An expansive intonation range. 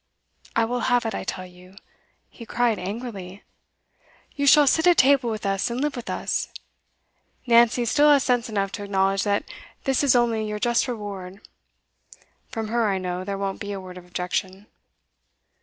No: average, 4.0 semitones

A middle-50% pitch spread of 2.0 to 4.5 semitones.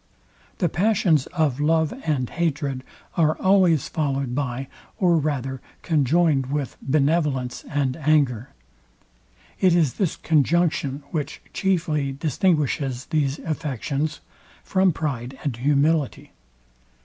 Yes: average, 3.3 semitones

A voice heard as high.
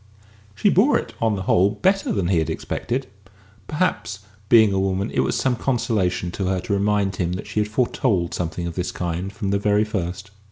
No: low, 100 Hz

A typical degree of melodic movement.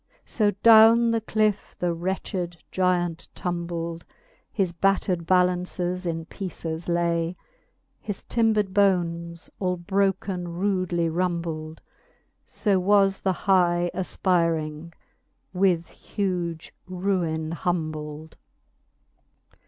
No: narrow, 2.3 semitones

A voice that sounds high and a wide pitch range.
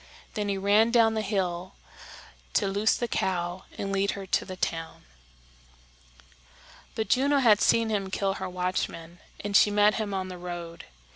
No: high, 195 Hz; average, 2.7 semitones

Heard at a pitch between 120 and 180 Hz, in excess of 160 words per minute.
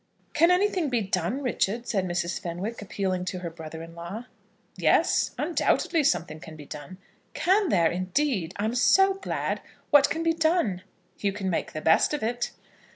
No: high, 205 Hz; average, 175 wpm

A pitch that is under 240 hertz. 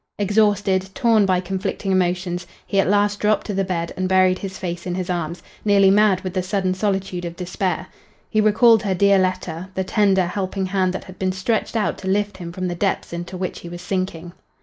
Yes: high, 190 Hz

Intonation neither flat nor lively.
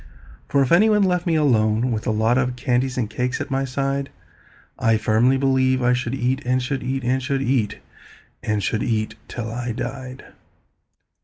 No: narrow, 2.3 semitones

